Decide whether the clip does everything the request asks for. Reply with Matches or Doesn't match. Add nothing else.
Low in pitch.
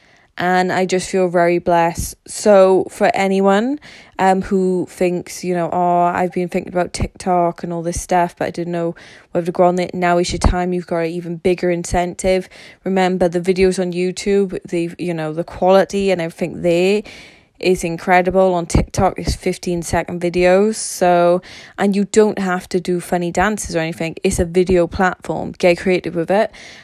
Doesn't match